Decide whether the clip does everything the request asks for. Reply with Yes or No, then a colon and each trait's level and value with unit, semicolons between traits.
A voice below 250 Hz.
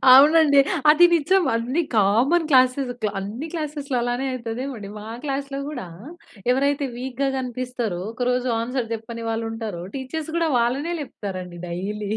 No: very high, 255 Hz